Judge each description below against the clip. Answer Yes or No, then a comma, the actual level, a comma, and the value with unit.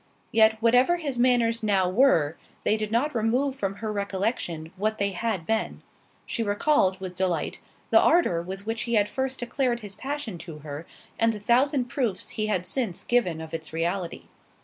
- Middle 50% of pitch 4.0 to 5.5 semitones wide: Yes, average, 4.7 semitones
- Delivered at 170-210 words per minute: Yes, average, 175 wpm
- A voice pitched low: No, high, 215 Hz